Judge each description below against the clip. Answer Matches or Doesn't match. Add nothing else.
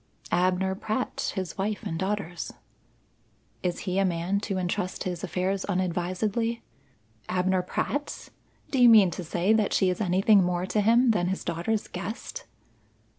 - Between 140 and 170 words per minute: Matches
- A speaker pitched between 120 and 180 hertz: Doesn't match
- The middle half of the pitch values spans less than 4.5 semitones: Matches